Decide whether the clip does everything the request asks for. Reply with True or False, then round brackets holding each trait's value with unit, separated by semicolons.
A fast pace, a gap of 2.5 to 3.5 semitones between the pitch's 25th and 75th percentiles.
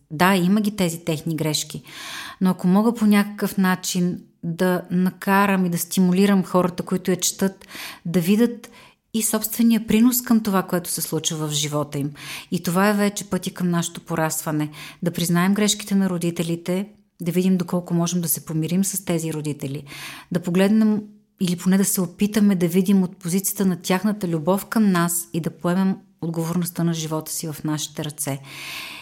True (170 wpm; 2.9 semitones)